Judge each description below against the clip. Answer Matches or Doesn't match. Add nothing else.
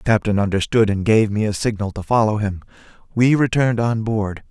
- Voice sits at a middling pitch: Doesn't match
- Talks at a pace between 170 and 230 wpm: Matches